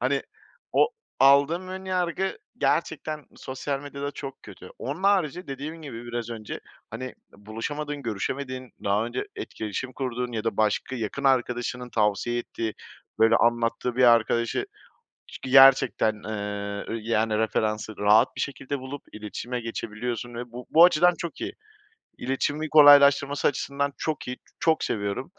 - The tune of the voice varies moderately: Yes, average, 4.0 semitones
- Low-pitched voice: Yes, low, 125 Hz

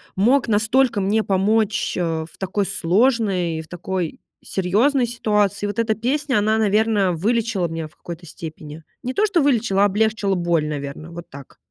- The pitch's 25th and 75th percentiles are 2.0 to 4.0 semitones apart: No, average, 4.5 semitones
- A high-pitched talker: Yes, high, 205 Hz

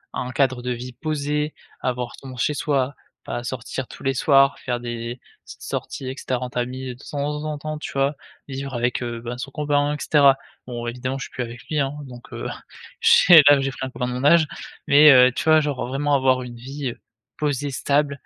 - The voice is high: No, low, 135 Hz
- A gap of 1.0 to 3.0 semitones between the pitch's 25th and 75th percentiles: Yes, average, 2.7 semitones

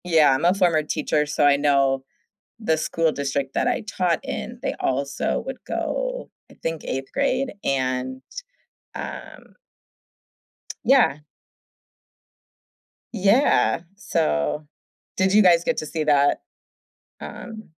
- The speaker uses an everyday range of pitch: No, wide, 6.3 semitones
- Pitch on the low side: No, medium, 160 Hz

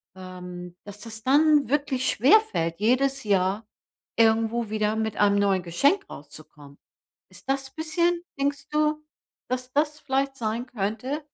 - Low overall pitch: No, high, 235 Hz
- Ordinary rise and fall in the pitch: No, wide, 5.8 semitones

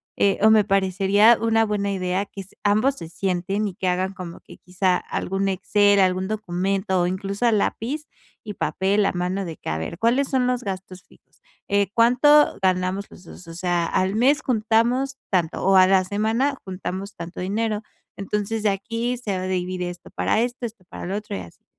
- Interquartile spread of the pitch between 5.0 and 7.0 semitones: No, average, 3.2 semitones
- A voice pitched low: No, high, 195 Hz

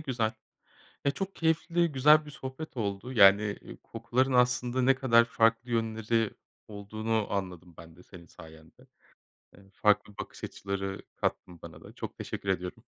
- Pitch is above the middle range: No, low, 115 Hz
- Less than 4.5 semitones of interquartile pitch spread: No, average, 4.8 semitones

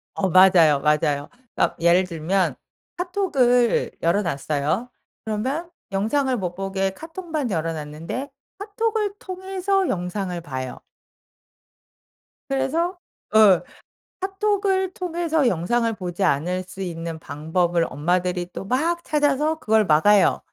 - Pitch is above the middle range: Yes, high, 200 Hz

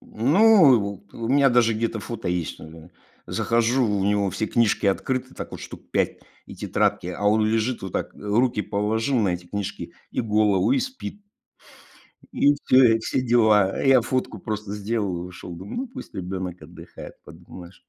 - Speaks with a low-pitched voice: Yes, low, 110 Hz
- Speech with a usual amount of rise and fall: Yes, average, 3.7 semitones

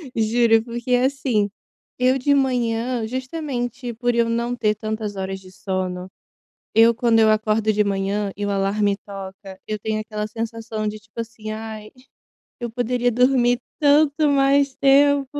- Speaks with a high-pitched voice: Yes, high, 225 Hz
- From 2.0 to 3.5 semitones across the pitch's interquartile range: Yes, average, 2.9 semitones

